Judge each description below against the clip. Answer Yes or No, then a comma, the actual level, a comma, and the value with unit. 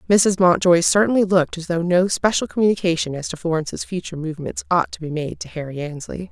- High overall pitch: No, medium, 175 Hz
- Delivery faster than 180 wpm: Yes, average, 200 wpm